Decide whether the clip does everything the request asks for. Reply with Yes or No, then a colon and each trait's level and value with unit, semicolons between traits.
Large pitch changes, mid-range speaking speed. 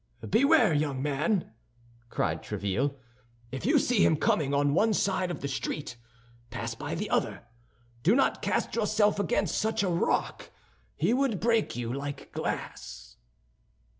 Yes: wide, 7.6 semitones; average, 150 wpm